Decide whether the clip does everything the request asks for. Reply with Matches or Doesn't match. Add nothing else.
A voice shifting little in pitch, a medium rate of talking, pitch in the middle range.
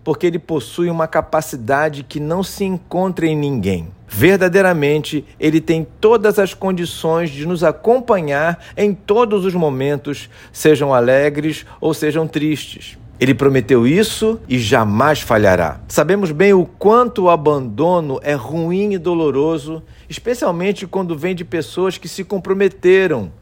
Doesn't match